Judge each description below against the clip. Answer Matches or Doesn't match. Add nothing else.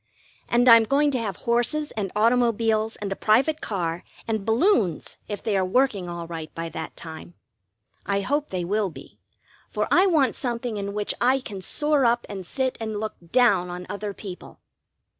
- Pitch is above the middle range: Matches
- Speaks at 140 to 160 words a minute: Doesn't match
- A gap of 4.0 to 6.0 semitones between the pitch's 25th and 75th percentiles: Matches